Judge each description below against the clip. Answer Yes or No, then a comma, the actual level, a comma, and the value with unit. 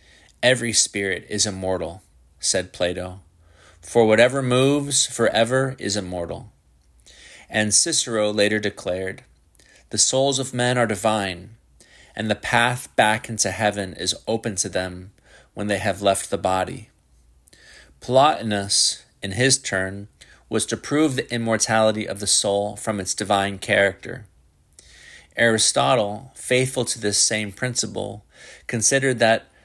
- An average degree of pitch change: Yes, average, 4.0 semitones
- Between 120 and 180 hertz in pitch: No, low, 105 Hz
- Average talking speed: No, slow, 125 wpm